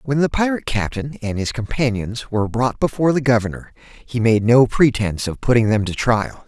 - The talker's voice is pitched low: Yes, low, 120 Hz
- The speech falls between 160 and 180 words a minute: No, average, 195 wpm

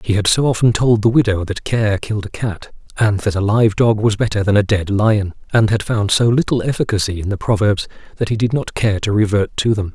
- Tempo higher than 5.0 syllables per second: Yes, 5.6 syllables/s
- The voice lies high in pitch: No, low, 105 Hz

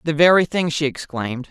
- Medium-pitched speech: Yes, medium, 150 Hz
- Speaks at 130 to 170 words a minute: No, average, 200 wpm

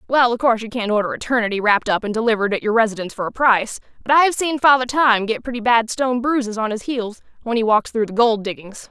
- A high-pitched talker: Yes, high, 230 Hz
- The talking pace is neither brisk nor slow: No, fast, 250 wpm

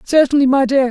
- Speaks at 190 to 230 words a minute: Yes, average, 200 wpm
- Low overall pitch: No, very high, 270 Hz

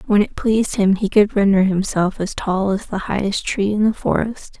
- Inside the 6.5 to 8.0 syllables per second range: No, 5.0 syllables/s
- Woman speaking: Yes, female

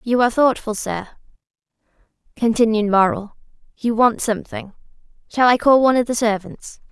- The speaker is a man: No, female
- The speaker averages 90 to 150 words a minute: Yes, average, 140 wpm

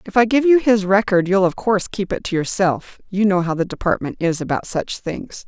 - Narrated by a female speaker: Yes, female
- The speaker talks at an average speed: No, fast, 240 wpm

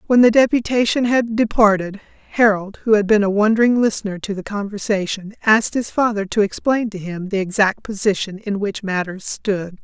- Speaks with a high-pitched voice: Yes, high, 210 Hz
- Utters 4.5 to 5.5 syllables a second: Yes, 5.4 syllables/s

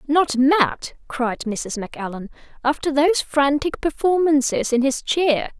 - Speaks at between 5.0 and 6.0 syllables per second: No, 4.1 syllables/s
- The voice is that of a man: No, female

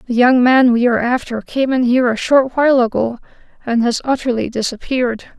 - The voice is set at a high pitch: Yes, high, 245 Hz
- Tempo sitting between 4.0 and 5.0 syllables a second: No, 5.9 syllables/s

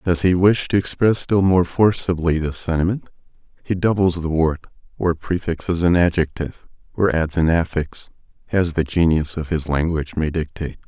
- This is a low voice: Yes, very low, 85 Hz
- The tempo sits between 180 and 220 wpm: No, average, 165 wpm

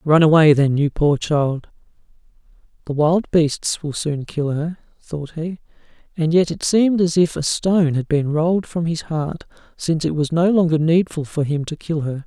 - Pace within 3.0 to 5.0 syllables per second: Yes, 4.7 syllables/s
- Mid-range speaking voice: Yes, medium, 155 Hz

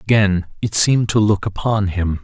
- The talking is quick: No, average, 190 wpm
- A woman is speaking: No, male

